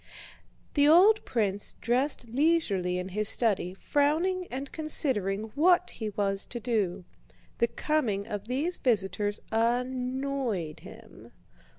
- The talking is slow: Yes, slow, 115 wpm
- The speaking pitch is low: No, high, 240 Hz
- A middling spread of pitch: No, wide, 6.1 semitones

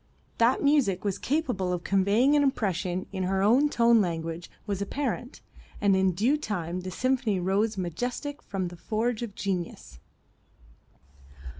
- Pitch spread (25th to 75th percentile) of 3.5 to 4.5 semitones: No, average, 5.0 semitones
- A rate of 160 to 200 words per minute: No, average, 145 wpm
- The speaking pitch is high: Yes, high, 200 Hz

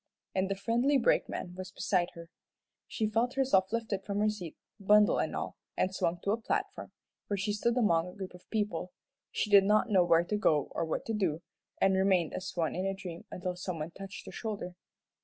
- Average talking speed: No, fast, 215 wpm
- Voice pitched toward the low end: No, high, 195 Hz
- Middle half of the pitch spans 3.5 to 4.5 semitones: No, average, 3.0 semitones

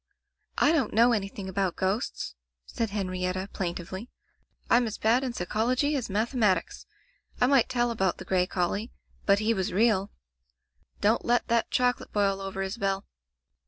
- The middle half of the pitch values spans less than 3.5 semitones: No, average, 3.8 semitones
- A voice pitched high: Yes, high, 210 Hz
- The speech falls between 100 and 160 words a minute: Yes, average, 150 wpm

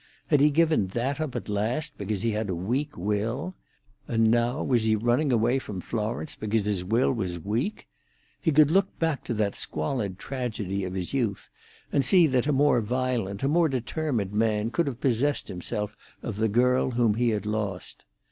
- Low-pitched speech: Yes, low, 115 Hz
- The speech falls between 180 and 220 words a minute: Yes, average, 190 wpm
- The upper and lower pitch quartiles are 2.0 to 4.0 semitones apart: No, average, 4.6 semitones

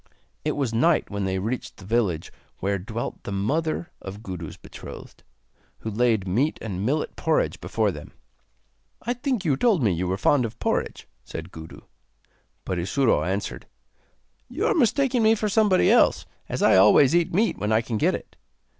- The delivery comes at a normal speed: Yes, average, 175 wpm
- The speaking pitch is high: No, low, 115 Hz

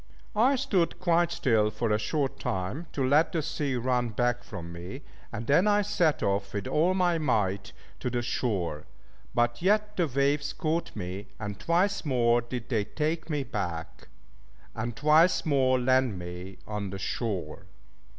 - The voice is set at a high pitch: No, low, 125 Hz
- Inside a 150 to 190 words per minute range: Yes, average, 165 wpm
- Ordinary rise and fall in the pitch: No, wide, 7.4 semitones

